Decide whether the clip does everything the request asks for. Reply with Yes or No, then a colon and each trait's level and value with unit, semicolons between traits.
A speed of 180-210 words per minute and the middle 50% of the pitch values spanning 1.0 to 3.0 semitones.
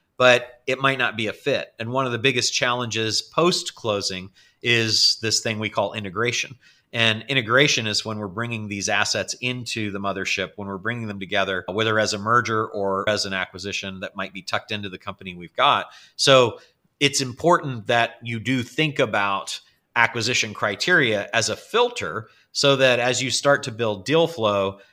No: average, 185 wpm; average, 3.9 semitones